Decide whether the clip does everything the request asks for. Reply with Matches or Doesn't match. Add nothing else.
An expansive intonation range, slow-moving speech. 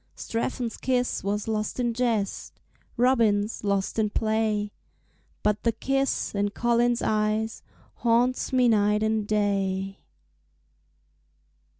Doesn't match